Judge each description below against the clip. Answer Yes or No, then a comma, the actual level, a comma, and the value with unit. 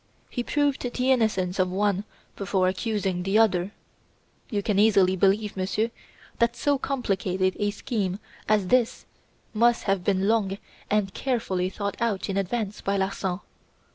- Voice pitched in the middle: No, high, 200 Hz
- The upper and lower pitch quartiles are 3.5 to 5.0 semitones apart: No, average, 3.1 semitones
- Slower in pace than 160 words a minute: Yes, average, 145 wpm